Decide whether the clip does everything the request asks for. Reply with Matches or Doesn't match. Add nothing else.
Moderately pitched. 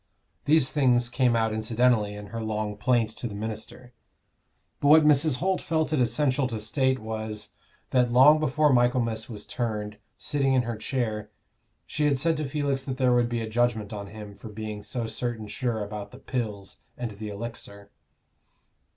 Doesn't match